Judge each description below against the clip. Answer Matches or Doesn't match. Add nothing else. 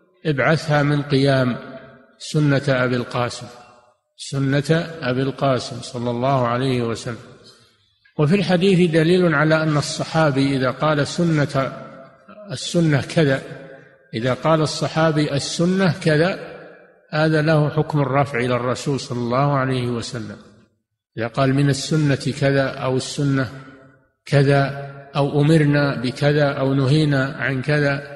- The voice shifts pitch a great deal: Doesn't match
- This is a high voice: Doesn't match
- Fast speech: Doesn't match